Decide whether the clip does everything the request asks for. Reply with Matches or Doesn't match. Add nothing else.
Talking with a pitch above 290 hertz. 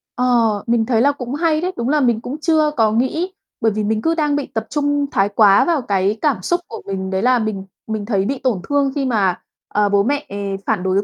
Doesn't match